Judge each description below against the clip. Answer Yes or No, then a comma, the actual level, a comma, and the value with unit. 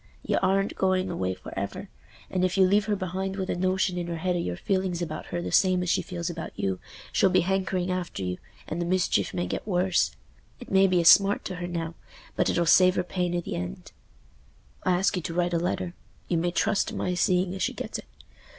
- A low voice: No, medium, 180 Hz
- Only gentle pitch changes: Yes, narrow, 1.5 semitones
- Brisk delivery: Yes, fast, 230 wpm